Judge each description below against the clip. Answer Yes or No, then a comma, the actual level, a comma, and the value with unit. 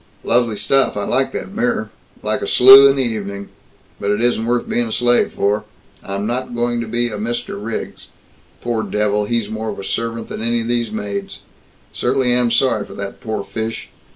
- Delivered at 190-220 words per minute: Yes, average, 200 wpm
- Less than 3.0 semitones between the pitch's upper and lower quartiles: Yes, narrow, 2.6 semitones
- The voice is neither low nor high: No, low, 115 Hz